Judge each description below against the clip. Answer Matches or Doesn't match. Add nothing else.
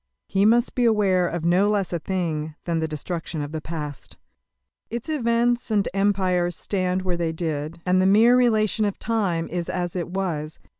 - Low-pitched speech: Doesn't match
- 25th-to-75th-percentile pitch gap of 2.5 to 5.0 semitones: Matches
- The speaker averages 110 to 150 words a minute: Doesn't match